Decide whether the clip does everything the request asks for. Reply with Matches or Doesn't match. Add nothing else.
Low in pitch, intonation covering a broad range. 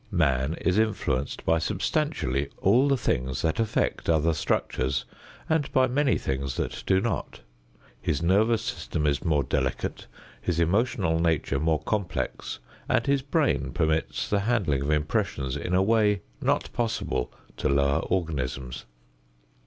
Matches